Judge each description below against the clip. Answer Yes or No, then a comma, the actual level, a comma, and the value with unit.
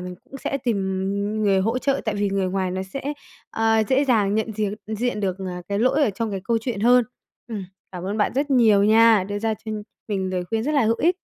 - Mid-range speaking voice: No, high, 215 Hz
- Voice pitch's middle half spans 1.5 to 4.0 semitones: Yes, average, 3.3 semitones